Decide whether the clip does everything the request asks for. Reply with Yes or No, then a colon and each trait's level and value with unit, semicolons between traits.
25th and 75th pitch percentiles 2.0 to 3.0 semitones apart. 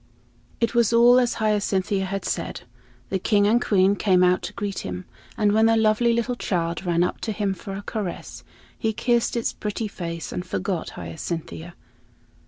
No: average, 3.6 semitones